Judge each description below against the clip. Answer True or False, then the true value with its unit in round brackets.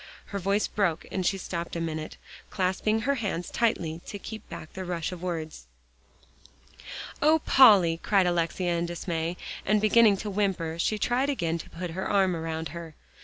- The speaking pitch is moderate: True (180 Hz)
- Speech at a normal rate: True (170 wpm)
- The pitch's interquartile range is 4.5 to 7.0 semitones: False (3.6 semitones)